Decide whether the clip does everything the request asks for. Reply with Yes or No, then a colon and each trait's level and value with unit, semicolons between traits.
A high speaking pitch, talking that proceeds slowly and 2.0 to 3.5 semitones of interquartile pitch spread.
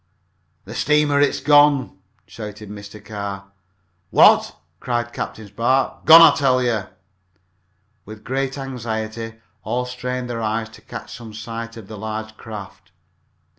No: low, 115 Hz; slow, 130 wpm; average, 2.9 semitones